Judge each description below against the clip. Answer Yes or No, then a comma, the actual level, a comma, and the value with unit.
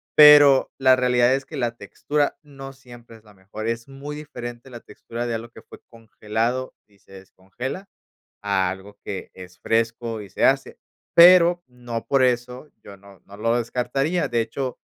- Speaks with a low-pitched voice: Yes, low, 120 Hz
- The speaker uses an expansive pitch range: No, average, 3.8 semitones